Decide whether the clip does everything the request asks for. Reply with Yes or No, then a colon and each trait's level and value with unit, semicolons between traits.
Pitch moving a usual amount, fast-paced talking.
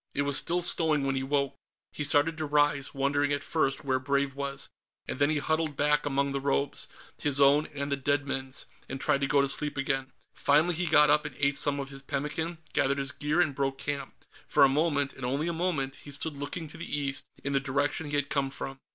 No: narrow, 1.3 semitones; fast, 235 wpm